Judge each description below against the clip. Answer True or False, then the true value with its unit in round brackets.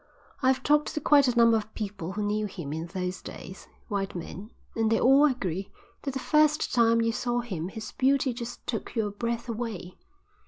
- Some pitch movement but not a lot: True (4.2 semitones)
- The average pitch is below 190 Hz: False (230 Hz)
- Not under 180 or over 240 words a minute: True (195 wpm)